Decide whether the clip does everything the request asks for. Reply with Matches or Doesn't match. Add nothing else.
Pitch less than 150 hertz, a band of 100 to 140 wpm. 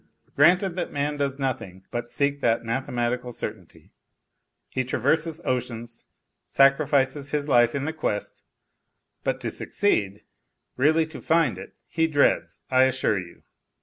Matches